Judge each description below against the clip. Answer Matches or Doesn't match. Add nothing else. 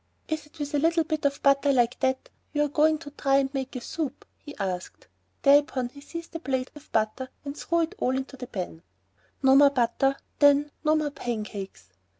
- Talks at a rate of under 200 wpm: Doesn't match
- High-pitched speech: Matches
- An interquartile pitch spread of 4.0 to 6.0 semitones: Doesn't match